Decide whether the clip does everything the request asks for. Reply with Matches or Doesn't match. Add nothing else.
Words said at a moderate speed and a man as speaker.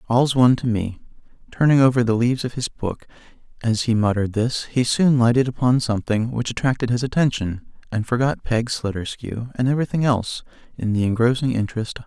Matches